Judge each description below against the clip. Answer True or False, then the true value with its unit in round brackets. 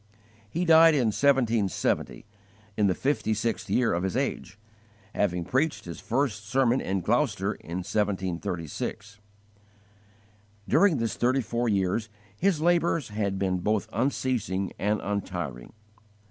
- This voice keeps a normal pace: False (125 wpm)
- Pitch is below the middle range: True (105 Hz)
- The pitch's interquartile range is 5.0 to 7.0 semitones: True (5.4 semitones)